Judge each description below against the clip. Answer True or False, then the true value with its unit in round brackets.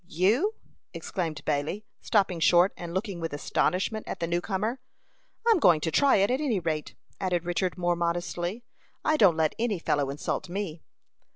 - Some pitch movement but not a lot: True (3.9 semitones)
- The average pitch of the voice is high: False (180 Hz)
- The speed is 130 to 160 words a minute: False (175 wpm)